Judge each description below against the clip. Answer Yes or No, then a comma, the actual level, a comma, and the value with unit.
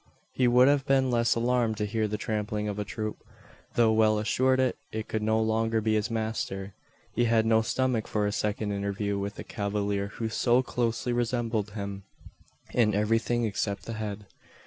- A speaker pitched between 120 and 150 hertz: No, low, 110 Hz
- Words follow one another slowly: No, average, 180 wpm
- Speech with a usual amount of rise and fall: No, narrow, 2.1 semitones